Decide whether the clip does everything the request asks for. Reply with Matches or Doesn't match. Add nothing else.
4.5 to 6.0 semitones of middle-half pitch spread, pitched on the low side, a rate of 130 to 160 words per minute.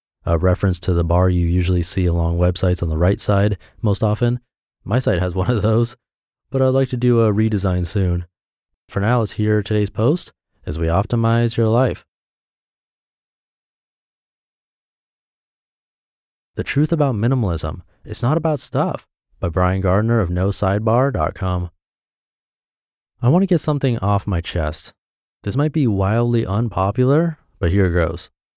Matches